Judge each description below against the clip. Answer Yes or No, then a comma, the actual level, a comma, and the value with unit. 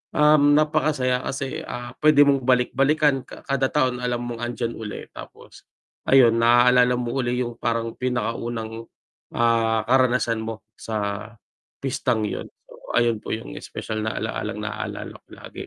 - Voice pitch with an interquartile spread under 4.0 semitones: Yes, narrow, 2.6 semitones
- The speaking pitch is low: Yes, low, 120 Hz